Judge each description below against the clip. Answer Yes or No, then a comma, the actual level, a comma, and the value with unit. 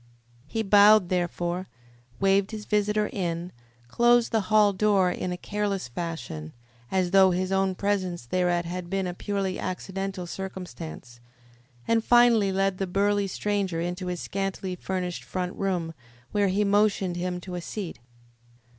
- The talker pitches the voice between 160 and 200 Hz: Yes, high, 190 Hz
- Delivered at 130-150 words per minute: Yes, average, 145 wpm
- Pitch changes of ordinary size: No, narrow, 2.3 semitones